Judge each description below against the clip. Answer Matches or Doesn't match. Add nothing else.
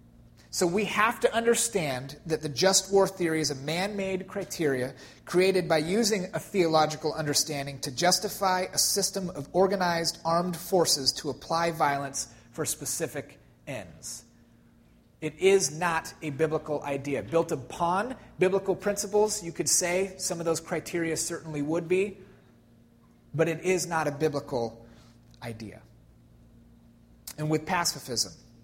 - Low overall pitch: Doesn't match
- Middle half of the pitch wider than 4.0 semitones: Matches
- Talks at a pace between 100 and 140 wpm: Matches